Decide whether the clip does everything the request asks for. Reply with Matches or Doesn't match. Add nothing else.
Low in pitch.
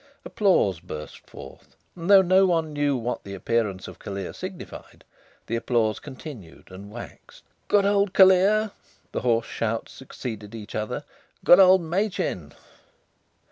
Matches